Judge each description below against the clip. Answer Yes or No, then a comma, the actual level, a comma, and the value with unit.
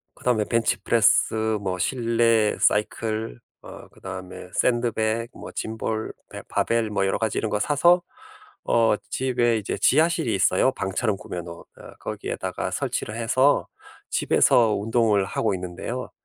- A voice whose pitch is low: Yes, low, 110 Hz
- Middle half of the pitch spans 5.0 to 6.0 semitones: No, average, 2.8 semitones